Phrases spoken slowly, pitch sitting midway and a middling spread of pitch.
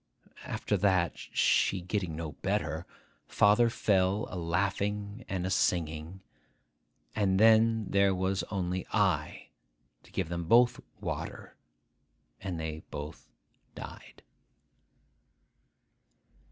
No: slow, 100 wpm; very low, 95 Hz; average, 3.3 semitones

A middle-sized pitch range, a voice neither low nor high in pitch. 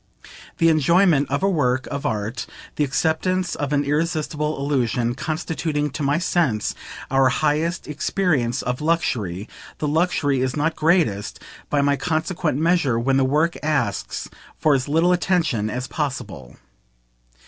Yes: average, 3.9 semitones; medium, 145 Hz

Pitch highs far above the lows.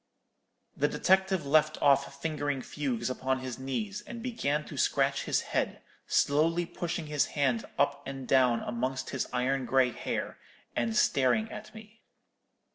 No: average, 4.5 semitones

